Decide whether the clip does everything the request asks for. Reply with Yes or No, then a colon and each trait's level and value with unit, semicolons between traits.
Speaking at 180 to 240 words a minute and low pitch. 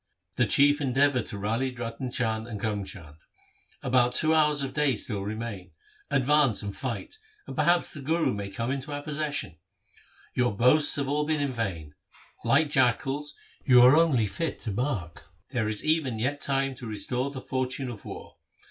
Yes: average, 185 wpm; low, 130 Hz